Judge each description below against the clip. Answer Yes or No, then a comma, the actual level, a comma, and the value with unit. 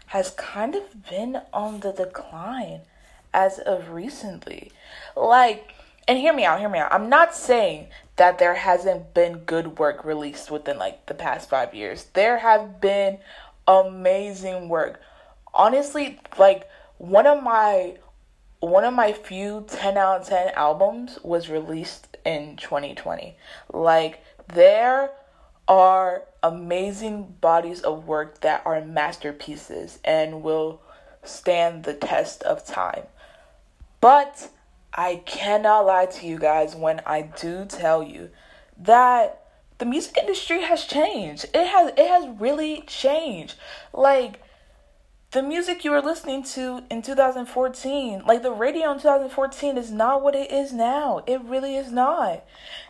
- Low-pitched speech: No, high, 210 Hz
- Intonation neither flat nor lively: No, wide, 8.1 semitones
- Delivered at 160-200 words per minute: No, average, 140 wpm